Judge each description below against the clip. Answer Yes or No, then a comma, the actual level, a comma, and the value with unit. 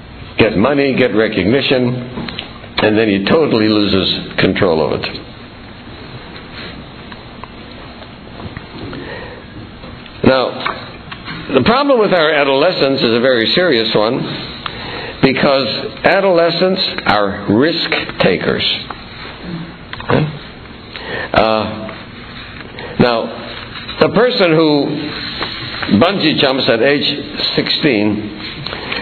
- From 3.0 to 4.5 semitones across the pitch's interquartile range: No, average, 5.1 semitones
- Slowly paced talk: Yes, slow, 80 wpm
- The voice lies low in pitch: Yes, low, 120 Hz